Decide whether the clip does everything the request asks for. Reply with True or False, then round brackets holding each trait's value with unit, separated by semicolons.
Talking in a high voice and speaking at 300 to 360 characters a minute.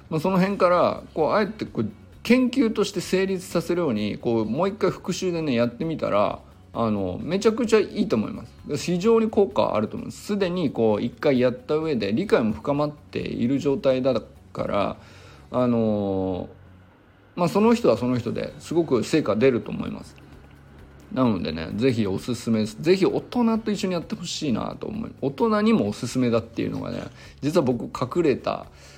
False (140 Hz; 350 characters per minute)